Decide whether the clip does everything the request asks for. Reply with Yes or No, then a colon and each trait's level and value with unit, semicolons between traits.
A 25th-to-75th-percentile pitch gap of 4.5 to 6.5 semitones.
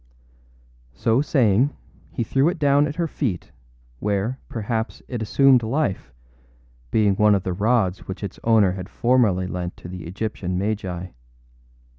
Yes: average, 5.1 semitones